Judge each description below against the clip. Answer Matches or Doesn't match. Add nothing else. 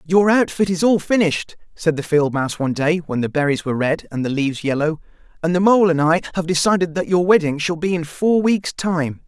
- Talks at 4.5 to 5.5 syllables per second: Doesn't match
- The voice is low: Doesn't match